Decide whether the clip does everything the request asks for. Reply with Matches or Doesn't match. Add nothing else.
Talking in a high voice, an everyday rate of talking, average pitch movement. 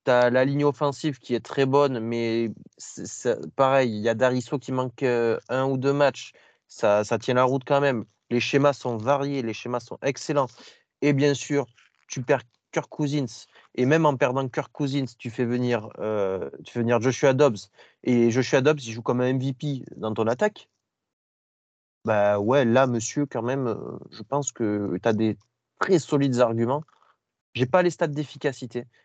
Doesn't match